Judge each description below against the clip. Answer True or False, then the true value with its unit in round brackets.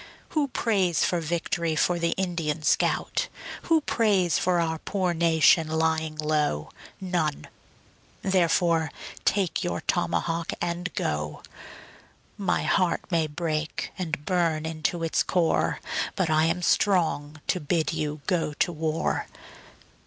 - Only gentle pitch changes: True (2.3 semitones)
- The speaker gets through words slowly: True (125 wpm)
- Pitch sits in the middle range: True (165 Hz)